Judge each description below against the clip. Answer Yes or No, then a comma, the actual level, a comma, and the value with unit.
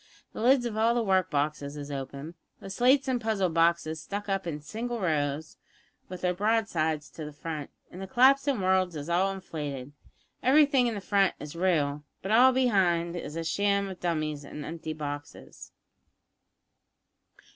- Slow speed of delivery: No, average, 160 wpm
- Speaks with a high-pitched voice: No, medium, 180 Hz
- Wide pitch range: Yes, wide, 6.1 semitones